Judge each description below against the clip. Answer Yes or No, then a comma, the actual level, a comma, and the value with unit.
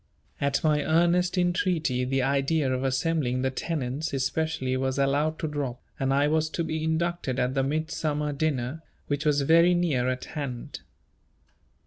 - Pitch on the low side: No, medium, 145 Hz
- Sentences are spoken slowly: No, average, 155 wpm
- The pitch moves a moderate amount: Yes, average, 3.3 semitones